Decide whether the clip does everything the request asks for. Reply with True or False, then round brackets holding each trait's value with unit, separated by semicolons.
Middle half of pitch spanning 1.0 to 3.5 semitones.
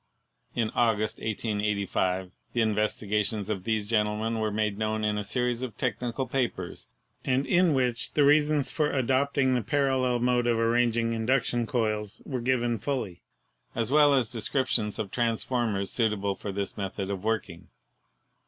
True (3.2 semitones)